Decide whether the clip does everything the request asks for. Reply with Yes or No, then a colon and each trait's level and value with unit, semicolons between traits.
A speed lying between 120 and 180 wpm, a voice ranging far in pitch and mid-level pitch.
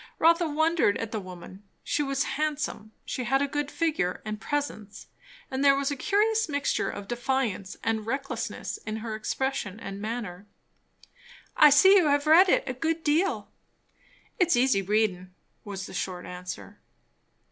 No: average, 160 wpm; wide, 6.3 semitones; very high, 265 Hz